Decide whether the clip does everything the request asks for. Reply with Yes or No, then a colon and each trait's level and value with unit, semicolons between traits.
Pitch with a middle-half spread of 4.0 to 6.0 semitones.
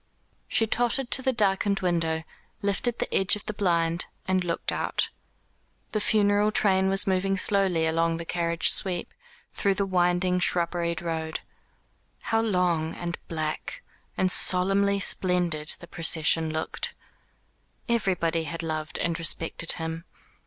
No: average, 3.0 semitones